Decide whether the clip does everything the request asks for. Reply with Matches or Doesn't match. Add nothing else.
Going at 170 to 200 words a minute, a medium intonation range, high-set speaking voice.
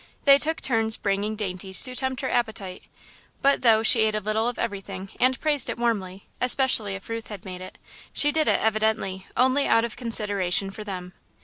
Matches